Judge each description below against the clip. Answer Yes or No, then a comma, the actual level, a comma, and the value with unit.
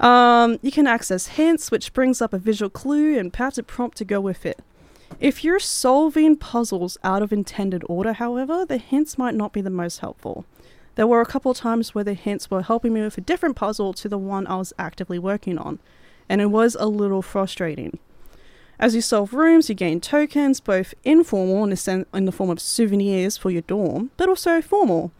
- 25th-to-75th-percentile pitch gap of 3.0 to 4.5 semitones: No, average, 5.2 semitones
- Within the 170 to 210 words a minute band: Yes, fast, 205 wpm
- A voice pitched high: Yes, high, 220 Hz